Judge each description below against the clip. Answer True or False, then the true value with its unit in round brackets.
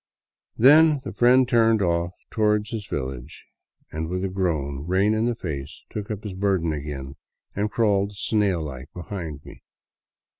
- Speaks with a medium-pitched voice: False (95 Hz)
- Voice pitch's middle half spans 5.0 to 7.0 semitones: True (5.5 semitones)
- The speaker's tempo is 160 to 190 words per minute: True (165 wpm)